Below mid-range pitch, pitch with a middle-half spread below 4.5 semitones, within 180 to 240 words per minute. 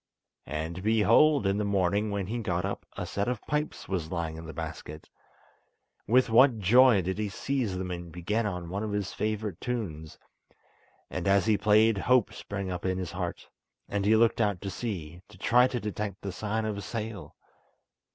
Yes: low, 100 Hz; average, 3.3 semitones; average, 190 wpm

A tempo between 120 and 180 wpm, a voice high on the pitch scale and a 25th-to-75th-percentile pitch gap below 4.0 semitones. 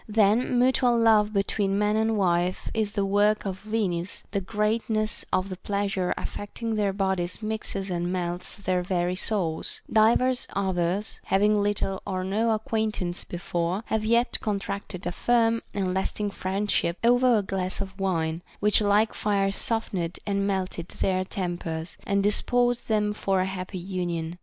Yes: average, 150 wpm; high, 200 Hz; average, 2.7 semitones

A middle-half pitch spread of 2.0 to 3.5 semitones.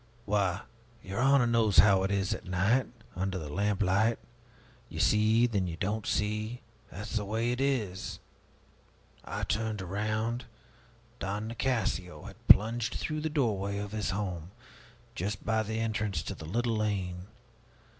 Yes: average, 2.9 semitones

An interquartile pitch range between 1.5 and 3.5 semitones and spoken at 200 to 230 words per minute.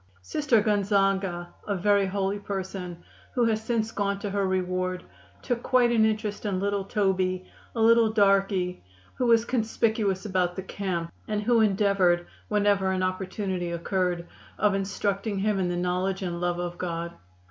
No: narrow, 2.4 semitones; average, 160 wpm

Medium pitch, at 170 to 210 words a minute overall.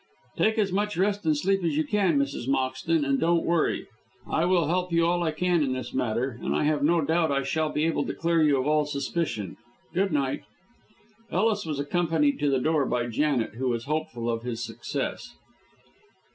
Yes: medium, 155 Hz; average, 200 wpm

